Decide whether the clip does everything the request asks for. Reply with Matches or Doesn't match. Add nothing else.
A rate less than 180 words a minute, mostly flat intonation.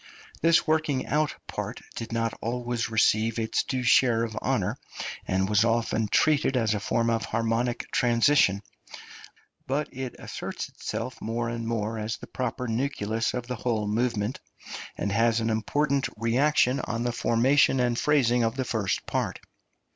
Matches